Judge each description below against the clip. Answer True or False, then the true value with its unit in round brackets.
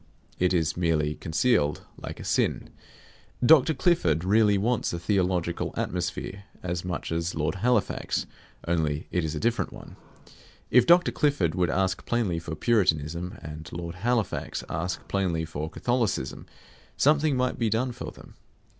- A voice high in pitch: False (90 Hz)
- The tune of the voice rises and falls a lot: True (6.2 semitones)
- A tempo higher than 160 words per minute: False (145 wpm)